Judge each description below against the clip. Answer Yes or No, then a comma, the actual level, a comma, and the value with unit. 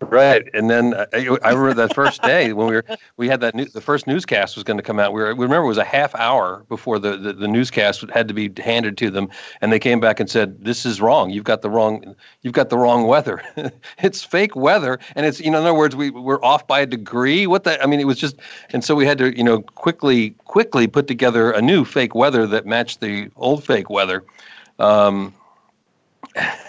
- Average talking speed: No, fast, 240 wpm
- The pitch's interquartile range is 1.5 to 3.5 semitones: No, average, 4.2 semitones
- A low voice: Yes, low, 120 Hz